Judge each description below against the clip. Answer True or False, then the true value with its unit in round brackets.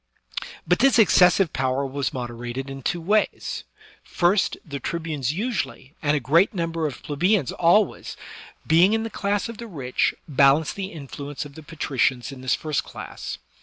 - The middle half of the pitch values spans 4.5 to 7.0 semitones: True (5.3 semitones)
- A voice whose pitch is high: False (155 Hz)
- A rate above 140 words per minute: True (165 wpm)